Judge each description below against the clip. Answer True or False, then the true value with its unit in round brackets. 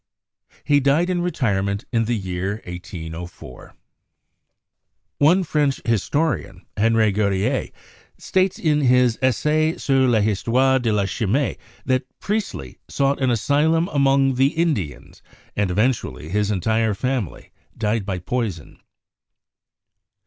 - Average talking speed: False (125 wpm)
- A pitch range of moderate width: False (6.0 semitones)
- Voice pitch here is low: True (120 Hz)